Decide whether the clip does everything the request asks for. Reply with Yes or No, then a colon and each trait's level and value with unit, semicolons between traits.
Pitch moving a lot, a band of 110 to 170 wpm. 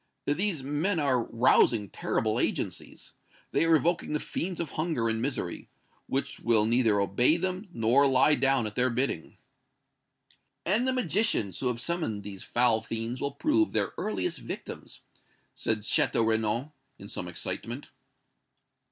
Yes: wide, 6.6 semitones; average, 145 wpm